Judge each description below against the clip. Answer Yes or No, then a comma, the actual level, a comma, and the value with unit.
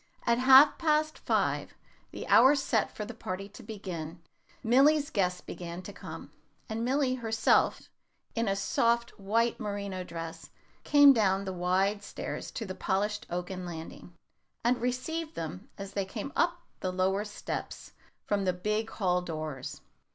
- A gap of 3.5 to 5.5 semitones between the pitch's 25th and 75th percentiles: Yes, average, 4.8 semitones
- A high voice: Yes, high, 205 Hz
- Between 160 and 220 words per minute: No, average, 150 wpm